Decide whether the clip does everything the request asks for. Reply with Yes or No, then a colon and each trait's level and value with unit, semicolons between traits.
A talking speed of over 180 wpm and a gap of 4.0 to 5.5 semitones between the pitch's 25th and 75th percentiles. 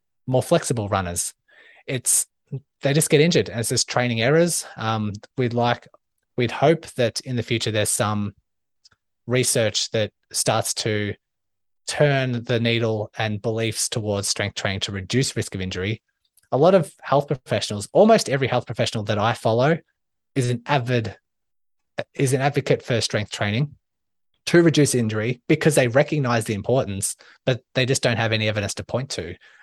No: average, 160 wpm; average, 4.4 semitones